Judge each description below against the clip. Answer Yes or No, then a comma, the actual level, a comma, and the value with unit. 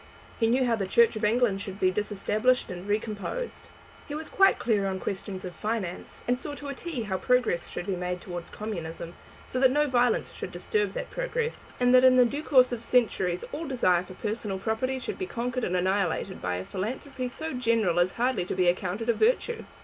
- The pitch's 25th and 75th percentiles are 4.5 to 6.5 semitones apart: Yes, average, 5.3 semitones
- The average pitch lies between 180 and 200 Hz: No, high, 225 Hz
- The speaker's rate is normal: No, fast, 210 wpm